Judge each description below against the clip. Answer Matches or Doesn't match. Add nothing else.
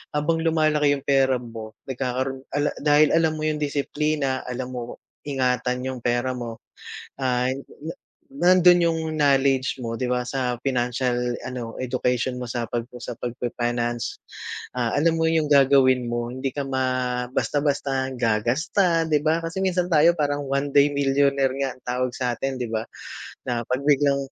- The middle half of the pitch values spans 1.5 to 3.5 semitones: Matches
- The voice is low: Matches